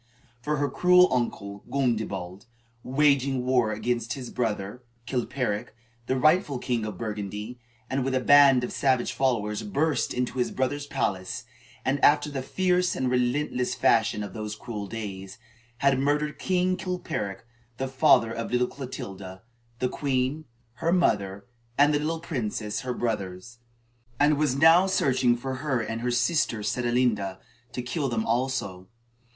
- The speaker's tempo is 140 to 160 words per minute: Yes, average, 145 wpm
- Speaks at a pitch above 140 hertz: No, low, 125 Hz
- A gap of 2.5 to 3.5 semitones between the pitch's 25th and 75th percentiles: No, average, 4.5 semitones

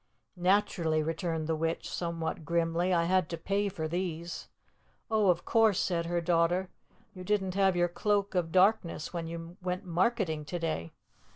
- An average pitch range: No, narrow, 2.2 semitones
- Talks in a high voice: No, medium, 175 Hz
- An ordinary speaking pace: Yes, average, 165 wpm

